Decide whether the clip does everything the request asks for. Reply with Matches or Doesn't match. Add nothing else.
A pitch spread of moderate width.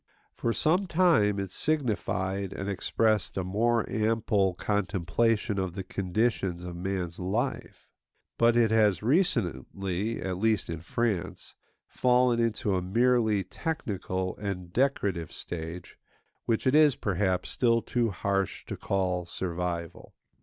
Matches